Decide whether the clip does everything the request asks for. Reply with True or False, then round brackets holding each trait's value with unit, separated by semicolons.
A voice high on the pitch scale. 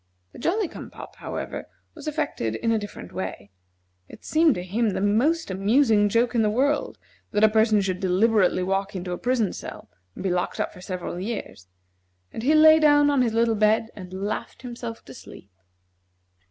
True (220 Hz)